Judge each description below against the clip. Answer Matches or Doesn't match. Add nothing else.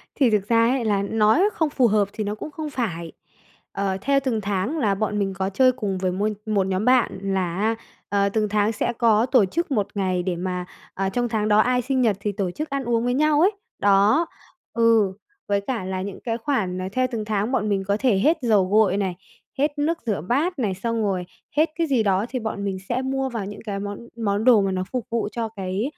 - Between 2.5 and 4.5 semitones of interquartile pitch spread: Matches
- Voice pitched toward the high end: Matches